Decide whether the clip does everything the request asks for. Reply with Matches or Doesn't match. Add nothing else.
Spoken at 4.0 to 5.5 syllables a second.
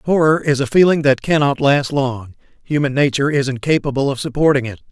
Doesn't match